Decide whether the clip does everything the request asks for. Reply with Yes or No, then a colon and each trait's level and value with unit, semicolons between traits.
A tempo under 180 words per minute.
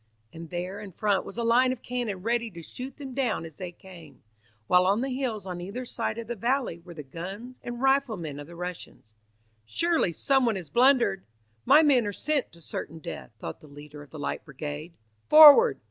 No: fast, 205 wpm